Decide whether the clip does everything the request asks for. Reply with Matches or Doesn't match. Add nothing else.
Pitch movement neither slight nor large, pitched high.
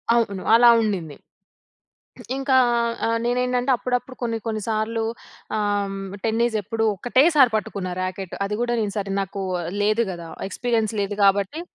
Matches